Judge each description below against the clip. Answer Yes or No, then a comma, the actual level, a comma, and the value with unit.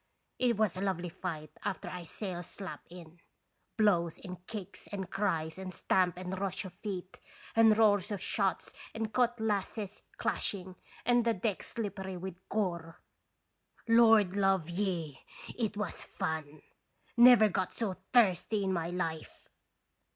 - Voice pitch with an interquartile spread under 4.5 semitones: Yes, average, 3.2 semitones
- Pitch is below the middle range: No, high, 190 Hz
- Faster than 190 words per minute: No, average, 140 wpm